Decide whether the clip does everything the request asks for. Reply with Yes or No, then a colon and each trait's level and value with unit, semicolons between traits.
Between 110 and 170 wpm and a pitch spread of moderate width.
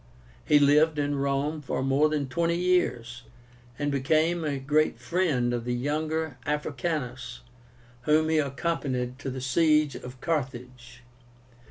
Yes: slow, 135 wpm; average, 3.5 semitones